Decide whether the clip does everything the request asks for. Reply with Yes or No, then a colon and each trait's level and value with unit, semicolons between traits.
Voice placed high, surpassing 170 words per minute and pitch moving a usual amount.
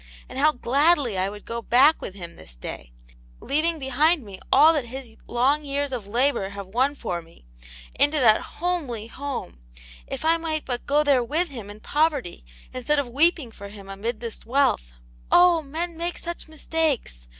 No: very high, 265 Hz; average, 180 wpm; wide, 6.0 semitones